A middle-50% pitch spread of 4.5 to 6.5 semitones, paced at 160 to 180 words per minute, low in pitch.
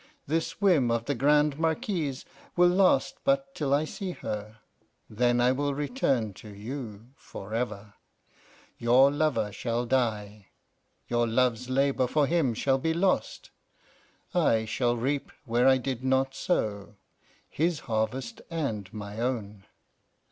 No: average, 4.8 semitones; slow, 135 wpm; low, 130 Hz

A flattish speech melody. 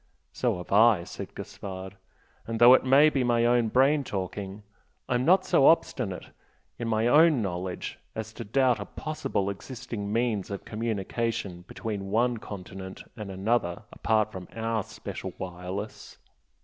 No: average, 3.7 semitones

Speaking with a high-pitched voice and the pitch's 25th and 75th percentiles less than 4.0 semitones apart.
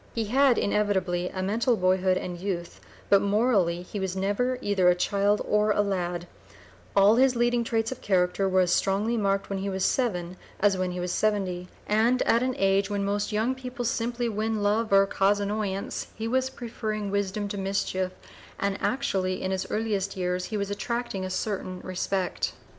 Yes: high, 200 Hz; average, 3.0 semitones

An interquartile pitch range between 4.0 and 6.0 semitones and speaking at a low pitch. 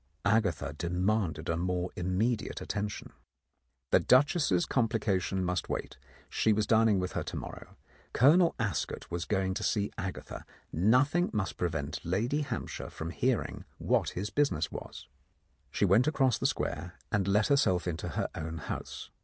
Yes: average, 4.4 semitones; low, 100 Hz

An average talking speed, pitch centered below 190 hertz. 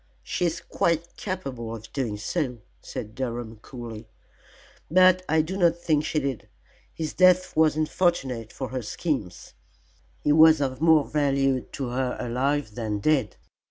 Yes: average, 150 wpm; medium, 140 Hz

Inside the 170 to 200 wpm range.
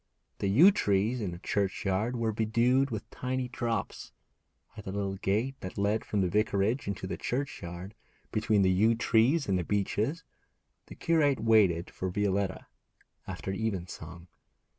No: average, 150 wpm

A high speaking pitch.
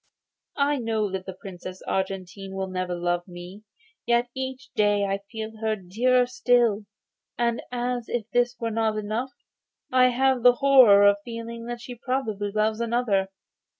Yes: high, 225 Hz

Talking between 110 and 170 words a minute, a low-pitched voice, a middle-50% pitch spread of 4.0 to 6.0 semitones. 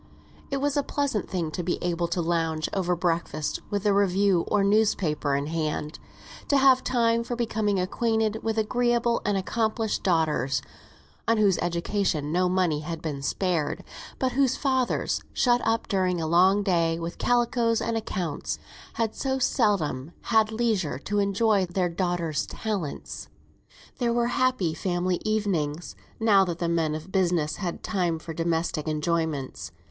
No: average, 155 wpm; medium, 185 Hz; average, 5.1 semitones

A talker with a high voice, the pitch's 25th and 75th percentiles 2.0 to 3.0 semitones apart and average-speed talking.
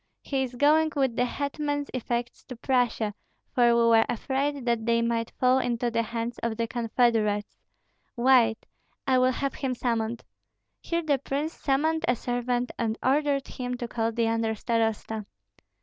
Yes: high, 245 Hz; average, 2.7 semitones; average, 165 wpm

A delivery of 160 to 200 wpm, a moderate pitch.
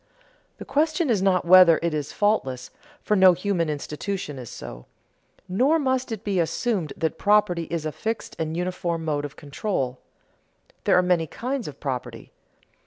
Yes: average, 165 wpm; medium, 180 Hz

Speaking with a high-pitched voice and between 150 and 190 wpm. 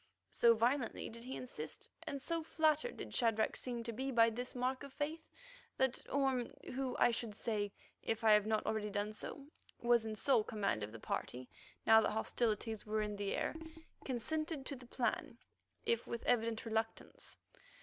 Yes: high, 235 Hz; average, 180 wpm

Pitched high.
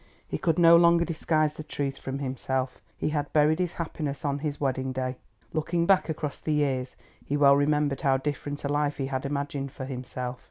No: medium, 145 Hz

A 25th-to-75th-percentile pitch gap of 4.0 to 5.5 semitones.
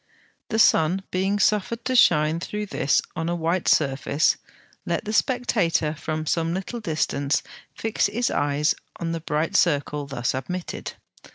Yes: average, 5.2 semitones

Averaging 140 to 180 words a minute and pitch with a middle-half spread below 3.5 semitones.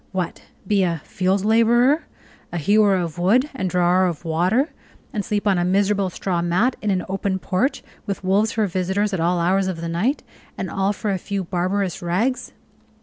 No: average, 190 wpm; average, 2.7 semitones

